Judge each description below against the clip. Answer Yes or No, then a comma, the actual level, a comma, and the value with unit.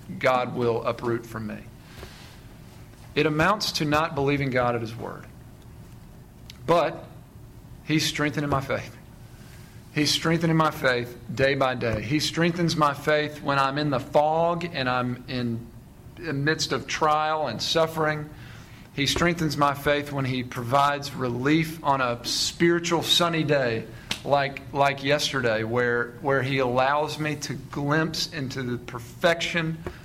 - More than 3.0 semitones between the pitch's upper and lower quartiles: Yes, average, 3.8 semitones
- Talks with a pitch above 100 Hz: Yes, medium, 140 Hz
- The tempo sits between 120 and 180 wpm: Yes, average, 140 wpm